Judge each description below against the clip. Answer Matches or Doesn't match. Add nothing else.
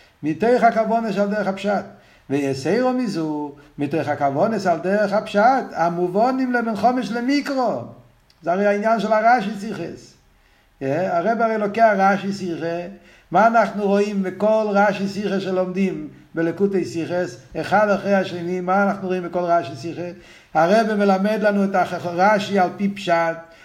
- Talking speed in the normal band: Matches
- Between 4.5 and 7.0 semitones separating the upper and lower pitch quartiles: Doesn't match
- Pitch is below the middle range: Doesn't match